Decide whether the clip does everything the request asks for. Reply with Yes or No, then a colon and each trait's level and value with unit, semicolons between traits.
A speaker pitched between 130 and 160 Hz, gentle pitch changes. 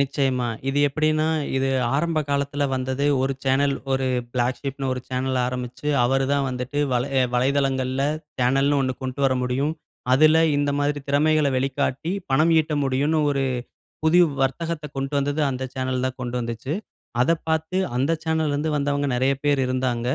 Yes: low, 135 Hz; narrow, 2.2 semitones